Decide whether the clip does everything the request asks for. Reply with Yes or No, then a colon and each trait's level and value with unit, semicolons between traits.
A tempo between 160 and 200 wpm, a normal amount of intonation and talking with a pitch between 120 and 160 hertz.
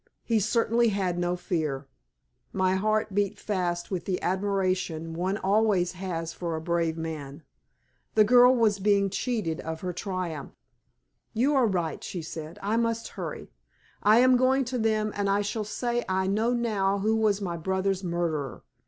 No: average, 165 wpm; average, 3.9 semitones; high, 195 Hz